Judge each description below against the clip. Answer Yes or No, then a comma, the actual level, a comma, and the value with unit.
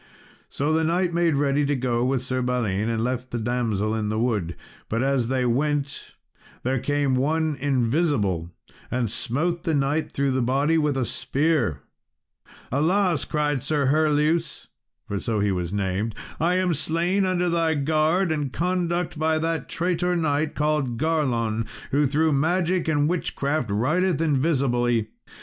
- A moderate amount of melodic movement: Yes, average, 4.8 semitones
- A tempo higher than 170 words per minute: No, average, 155 wpm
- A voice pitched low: No, medium, 145 Hz